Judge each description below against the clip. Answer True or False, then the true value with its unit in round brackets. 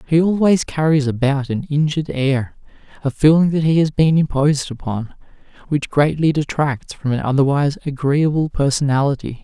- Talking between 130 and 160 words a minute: True (145 wpm)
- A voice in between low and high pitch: True (145 Hz)